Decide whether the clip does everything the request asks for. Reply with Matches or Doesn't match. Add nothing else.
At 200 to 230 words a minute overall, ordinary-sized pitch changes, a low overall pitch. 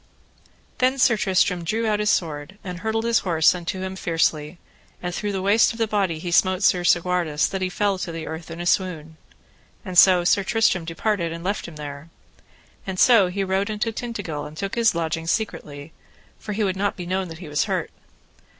Doesn't match